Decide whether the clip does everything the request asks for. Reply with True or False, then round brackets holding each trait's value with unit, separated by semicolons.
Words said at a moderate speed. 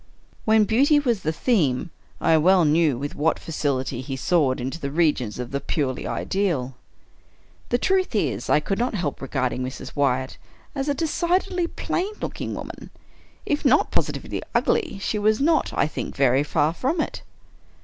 True (165 wpm)